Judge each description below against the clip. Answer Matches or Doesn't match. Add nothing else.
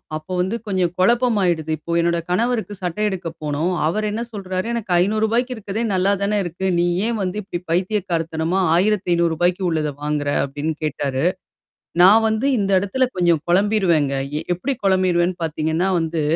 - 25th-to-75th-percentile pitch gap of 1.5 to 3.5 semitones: Doesn't match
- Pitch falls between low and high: Matches